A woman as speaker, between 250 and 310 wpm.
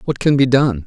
No: male; fast, 280 wpm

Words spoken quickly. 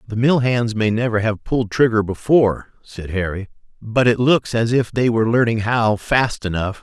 No: average, 195 wpm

